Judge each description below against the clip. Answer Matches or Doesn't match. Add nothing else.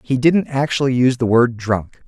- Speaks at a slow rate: Doesn't match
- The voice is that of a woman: Doesn't match